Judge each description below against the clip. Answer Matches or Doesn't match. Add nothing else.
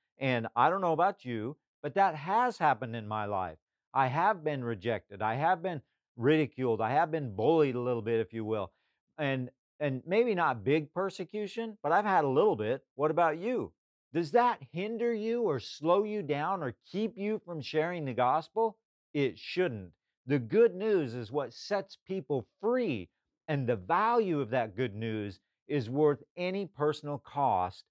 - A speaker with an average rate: Matches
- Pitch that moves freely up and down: Matches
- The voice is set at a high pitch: Doesn't match